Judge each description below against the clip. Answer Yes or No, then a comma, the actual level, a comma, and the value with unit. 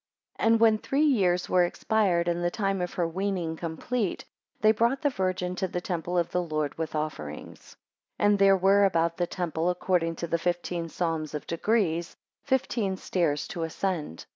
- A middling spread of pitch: Yes, average, 3.0 semitones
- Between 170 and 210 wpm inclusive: Yes, average, 180 wpm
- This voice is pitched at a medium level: Yes, medium, 180 Hz